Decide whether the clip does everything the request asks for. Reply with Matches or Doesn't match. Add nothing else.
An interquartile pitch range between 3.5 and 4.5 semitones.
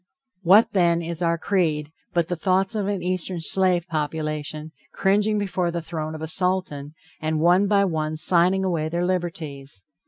Doesn't match